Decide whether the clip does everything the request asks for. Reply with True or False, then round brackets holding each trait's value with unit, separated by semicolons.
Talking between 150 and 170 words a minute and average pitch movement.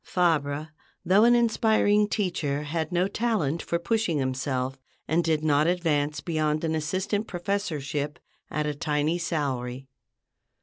False (135 wpm; 4.0 semitones)